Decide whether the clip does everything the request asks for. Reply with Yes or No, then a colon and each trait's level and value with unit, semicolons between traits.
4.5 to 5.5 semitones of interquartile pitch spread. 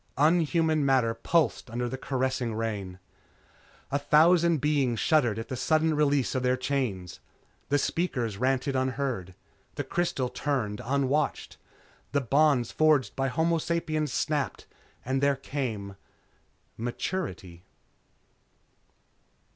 No: average, 4.0 semitones